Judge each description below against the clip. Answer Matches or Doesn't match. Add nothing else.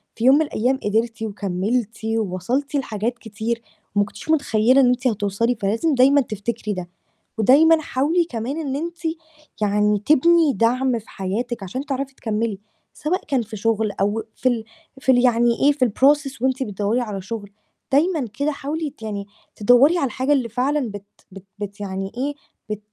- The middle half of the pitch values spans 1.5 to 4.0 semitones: Doesn't match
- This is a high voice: Matches